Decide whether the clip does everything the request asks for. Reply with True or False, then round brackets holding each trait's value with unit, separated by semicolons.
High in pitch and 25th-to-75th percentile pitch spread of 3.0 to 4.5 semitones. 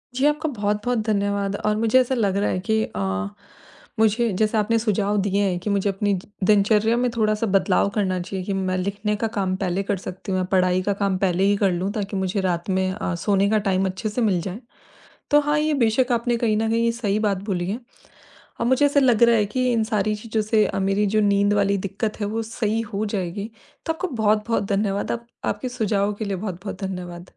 False (205 Hz; 2.6 semitones)